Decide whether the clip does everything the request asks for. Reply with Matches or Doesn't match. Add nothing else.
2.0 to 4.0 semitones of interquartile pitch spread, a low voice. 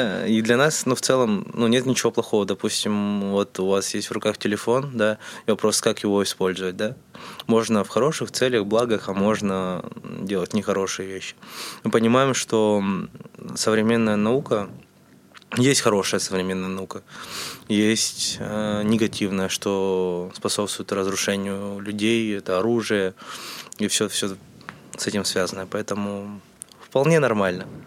Matches